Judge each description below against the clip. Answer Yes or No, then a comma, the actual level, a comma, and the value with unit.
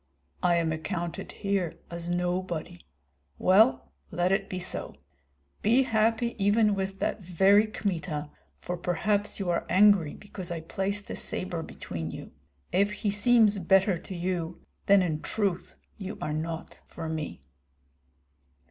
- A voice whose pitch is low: No, medium, 185 Hz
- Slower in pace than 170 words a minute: Yes, average, 140 wpm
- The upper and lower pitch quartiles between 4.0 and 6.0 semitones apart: No, average, 3.2 semitones